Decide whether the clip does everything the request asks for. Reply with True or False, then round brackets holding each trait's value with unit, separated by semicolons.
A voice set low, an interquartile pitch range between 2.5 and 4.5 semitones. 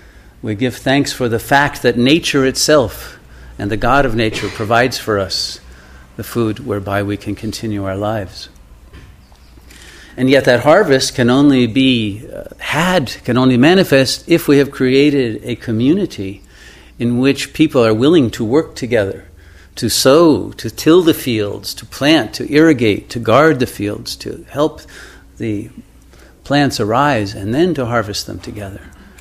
False (115 Hz; 4.9 semitones)